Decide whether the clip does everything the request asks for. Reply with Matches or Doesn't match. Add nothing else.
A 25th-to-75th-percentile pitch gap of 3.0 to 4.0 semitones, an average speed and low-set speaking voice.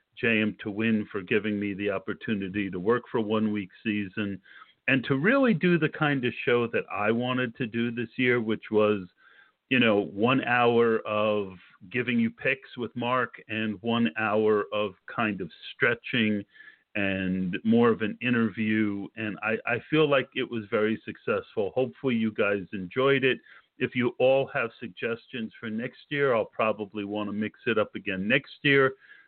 Matches